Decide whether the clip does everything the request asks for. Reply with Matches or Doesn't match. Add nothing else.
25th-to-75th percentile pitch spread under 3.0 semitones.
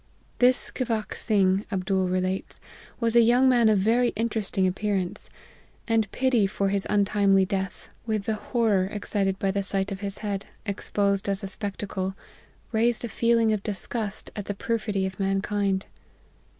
Matches